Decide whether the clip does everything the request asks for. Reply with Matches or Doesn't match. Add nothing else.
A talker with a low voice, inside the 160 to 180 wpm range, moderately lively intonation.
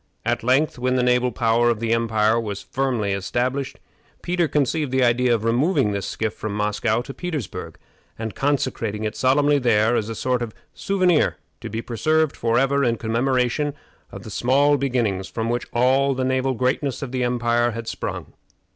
Matches